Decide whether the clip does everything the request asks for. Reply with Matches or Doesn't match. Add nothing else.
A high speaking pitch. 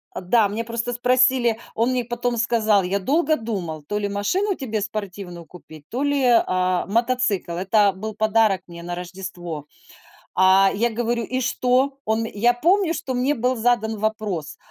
Matches